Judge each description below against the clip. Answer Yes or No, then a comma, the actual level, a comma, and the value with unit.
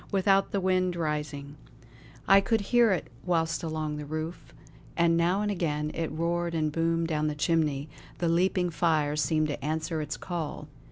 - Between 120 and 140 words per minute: No, average, 175 wpm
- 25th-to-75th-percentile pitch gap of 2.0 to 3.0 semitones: Yes, average, 2.7 semitones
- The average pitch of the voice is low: No, medium, 165 Hz